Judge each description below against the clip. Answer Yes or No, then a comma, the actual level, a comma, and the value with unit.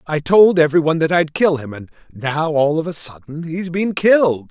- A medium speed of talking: No, fast, 225 wpm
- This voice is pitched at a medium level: Yes, medium, 160 Hz